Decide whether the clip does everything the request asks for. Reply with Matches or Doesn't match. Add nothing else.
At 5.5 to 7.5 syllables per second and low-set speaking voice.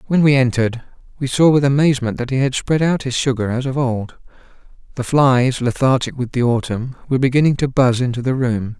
Matches